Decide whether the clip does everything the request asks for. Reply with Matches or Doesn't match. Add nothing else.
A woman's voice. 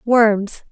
Matches